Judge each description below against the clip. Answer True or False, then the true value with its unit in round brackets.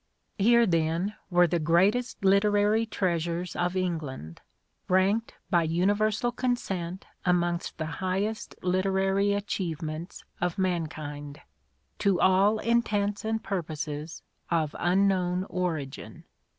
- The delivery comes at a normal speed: False (100 wpm)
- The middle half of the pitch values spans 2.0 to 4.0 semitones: True (3.3 semitones)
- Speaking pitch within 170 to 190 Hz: True (185 Hz)